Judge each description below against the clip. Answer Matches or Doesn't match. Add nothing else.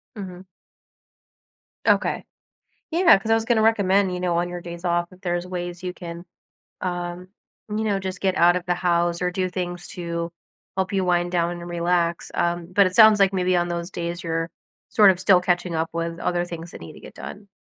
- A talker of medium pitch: Matches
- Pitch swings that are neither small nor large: Doesn't match